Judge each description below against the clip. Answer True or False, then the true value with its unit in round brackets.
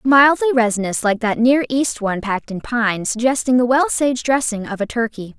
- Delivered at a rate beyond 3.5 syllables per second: True (5.3 syllables/s)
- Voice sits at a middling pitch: False (240 Hz)